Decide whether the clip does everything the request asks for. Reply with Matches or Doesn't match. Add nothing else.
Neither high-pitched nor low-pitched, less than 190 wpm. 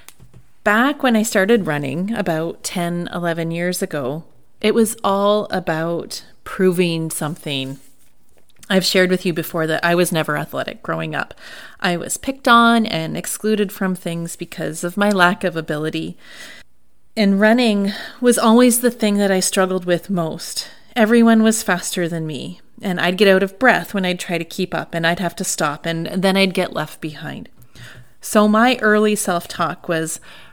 Matches